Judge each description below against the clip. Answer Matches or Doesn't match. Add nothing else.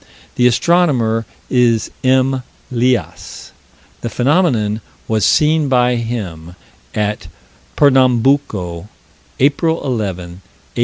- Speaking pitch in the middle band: Doesn't match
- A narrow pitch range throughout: Doesn't match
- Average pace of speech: Doesn't match